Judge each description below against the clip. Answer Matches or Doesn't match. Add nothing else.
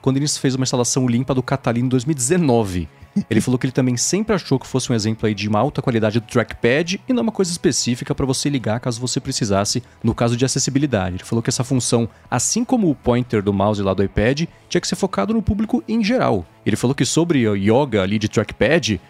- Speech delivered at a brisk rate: Matches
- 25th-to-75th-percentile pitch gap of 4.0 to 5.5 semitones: Matches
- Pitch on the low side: Matches